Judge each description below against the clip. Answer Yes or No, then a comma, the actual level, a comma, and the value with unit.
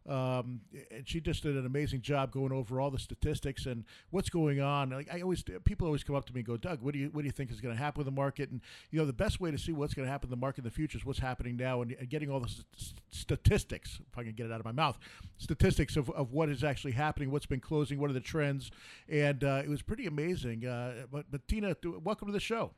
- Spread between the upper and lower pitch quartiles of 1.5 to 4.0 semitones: Yes, average, 3.0 semitones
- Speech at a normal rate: No, fast, 285 wpm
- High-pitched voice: No, medium, 140 Hz